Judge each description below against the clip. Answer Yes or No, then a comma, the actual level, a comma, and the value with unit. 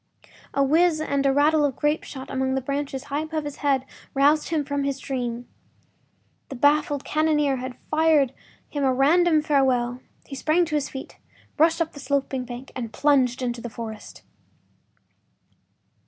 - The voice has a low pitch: No, very high, 280 Hz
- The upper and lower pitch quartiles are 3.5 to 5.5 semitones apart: No, narrow, 2.5 semitones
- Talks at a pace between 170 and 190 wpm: No, average, 160 wpm